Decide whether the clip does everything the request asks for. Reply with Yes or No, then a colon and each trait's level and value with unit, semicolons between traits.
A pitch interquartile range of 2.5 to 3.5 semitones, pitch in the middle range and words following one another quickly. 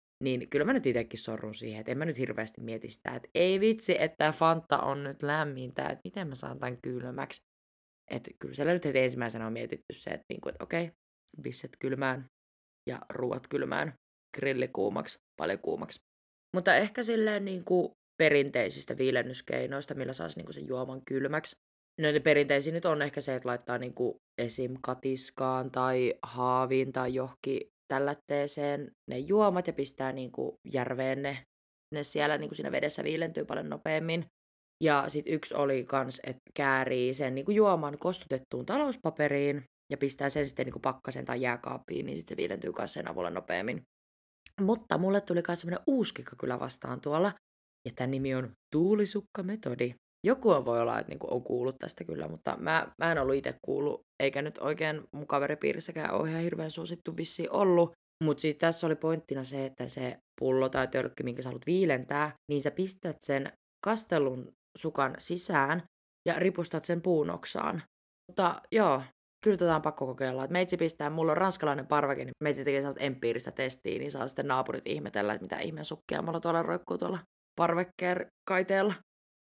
No: average, 4.5 semitones; medium, 145 Hz; fast, 175 wpm